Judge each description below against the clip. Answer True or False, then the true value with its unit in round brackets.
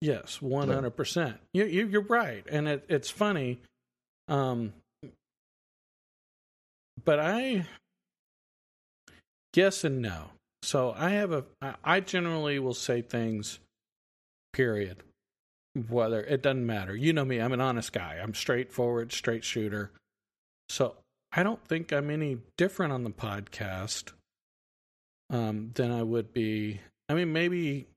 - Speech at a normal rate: False (130 wpm)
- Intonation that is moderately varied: False (5.9 semitones)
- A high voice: False (125 Hz)